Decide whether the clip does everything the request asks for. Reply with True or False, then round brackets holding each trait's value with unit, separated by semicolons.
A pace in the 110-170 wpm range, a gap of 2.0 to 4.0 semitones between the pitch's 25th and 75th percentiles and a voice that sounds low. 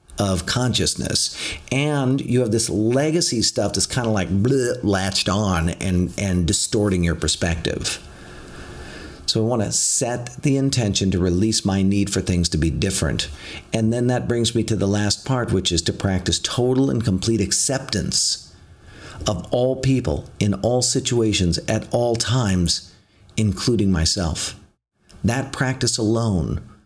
False (150 wpm; 4.7 semitones; 105 Hz)